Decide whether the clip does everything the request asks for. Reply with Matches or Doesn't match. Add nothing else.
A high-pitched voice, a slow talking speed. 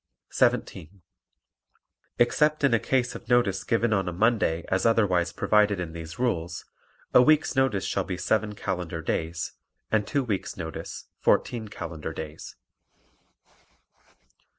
Doesn't match